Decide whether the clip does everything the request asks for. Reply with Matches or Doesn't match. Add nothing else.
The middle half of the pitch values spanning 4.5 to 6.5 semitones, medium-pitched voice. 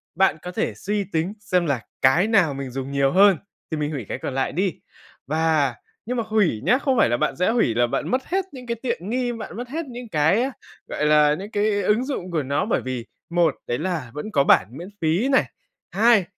Doesn't match